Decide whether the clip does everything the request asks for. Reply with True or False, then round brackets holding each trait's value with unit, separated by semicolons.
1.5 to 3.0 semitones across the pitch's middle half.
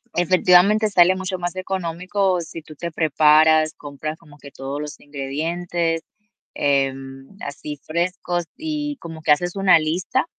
False (3.5 semitones)